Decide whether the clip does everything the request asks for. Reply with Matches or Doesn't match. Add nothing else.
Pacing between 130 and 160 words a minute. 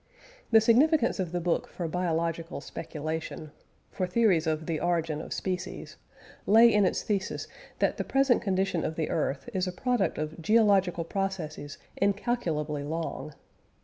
Matches